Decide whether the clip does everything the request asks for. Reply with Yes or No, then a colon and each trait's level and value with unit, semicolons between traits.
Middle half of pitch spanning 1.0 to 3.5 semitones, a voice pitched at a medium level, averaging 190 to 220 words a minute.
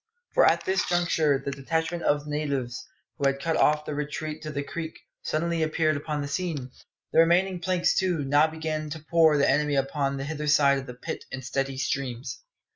Yes: average, 2.7 semitones; medium, 150 Hz; average, 200 wpm